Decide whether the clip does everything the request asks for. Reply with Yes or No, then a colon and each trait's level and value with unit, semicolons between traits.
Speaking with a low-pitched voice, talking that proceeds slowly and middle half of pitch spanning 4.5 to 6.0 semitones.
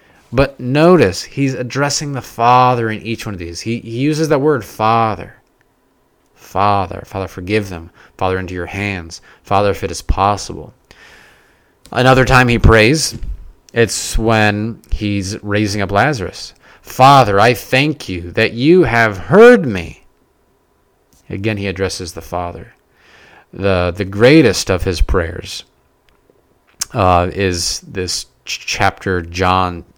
Yes: low, 105 Hz; slow, 130 wpm; average, 5.0 semitones